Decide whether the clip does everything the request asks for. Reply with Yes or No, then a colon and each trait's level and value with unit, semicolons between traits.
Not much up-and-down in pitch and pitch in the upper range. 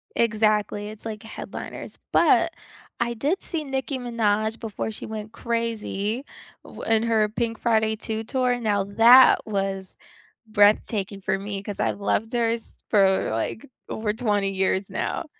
Yes: narrow, 2.2 semitones; high, 220 Hz